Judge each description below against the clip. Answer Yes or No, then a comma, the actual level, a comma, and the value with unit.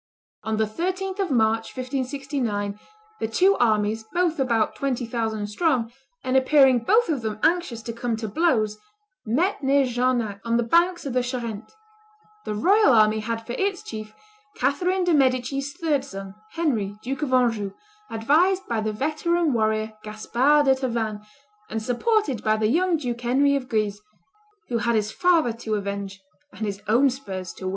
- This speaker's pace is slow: No, average, 170 wpm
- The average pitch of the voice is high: Yes, high, 245 Hz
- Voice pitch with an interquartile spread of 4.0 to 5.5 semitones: Yes, average, 4.8 semitones